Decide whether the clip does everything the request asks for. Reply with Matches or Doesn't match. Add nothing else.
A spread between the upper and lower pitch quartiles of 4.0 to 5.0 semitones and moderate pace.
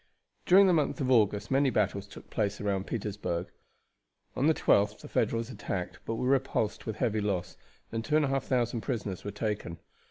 Matches